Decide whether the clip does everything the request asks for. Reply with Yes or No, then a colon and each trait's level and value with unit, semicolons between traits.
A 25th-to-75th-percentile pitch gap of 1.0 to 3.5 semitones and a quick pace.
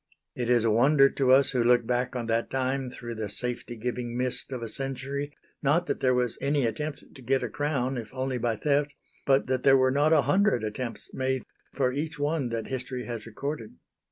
Yes: narrow, 2.5 semitones; fast, 215 wpm